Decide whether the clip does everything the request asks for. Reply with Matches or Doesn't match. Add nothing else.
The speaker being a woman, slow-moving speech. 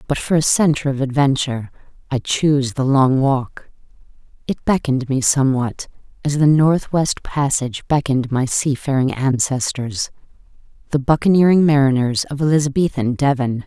Matches